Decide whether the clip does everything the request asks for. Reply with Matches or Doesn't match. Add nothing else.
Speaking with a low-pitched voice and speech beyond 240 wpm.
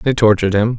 Doesn't match